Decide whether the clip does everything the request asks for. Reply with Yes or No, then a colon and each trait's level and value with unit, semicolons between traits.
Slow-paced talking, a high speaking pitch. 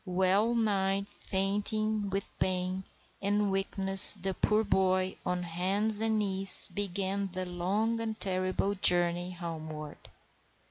Yes: slow, 120 wpm; high, 195 Hz